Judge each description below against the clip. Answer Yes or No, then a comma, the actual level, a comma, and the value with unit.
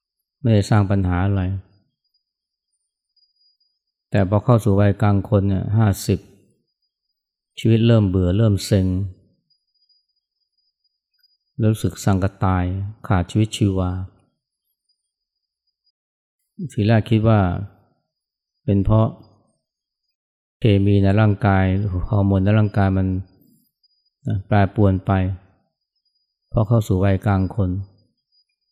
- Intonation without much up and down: Yes, narrow, 2.3 semitones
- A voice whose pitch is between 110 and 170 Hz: No, low, 100 Hz